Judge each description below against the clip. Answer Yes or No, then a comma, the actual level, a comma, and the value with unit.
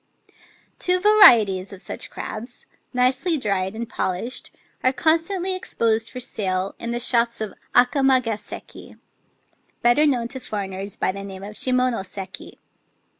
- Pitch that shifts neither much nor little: Yes, average, 4.6 semitones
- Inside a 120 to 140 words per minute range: Yes, slow, 135 wpm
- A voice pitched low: No, high, 235 Hz